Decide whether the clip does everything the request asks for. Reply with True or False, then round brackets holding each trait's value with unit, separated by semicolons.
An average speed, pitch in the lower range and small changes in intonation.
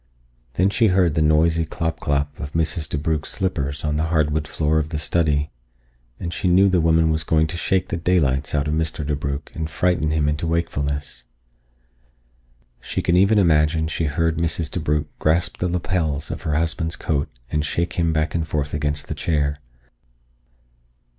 True (175 wpm; 80 Hz; 2.1 semitones)